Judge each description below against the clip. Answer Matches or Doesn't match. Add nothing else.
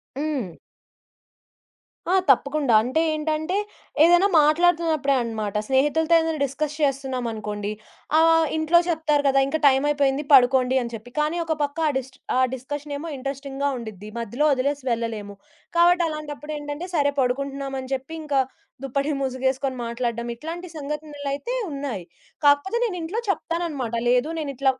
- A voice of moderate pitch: Doesn't match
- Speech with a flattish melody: Doesn't match